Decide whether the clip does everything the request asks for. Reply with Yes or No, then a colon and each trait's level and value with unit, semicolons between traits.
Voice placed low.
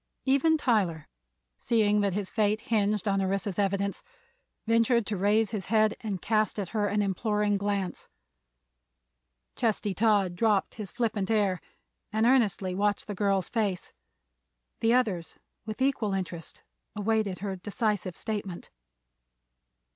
No: high, 205 Hz